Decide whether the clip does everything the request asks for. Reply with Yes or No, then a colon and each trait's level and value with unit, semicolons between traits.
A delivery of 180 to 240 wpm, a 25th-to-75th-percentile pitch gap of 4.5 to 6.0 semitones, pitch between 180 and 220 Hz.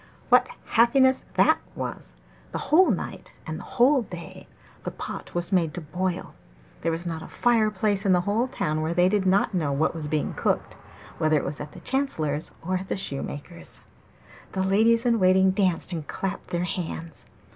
Yes: average, 190 wpm; average, 4.8 semitones; medium, 185 Hz